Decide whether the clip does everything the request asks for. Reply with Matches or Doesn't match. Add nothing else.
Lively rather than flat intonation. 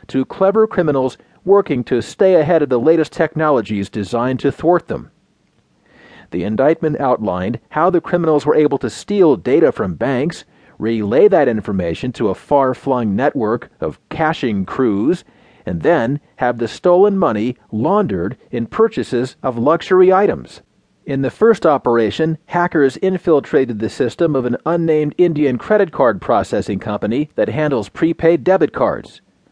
Matches